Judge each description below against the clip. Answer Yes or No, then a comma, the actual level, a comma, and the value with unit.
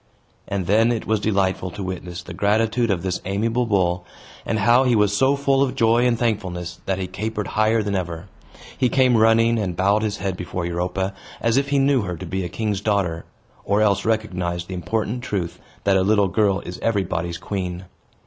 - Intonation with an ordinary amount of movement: Yes, average, 3.6 semitones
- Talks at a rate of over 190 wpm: Yes, average, 200 wpm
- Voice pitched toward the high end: No, low, 100 Hz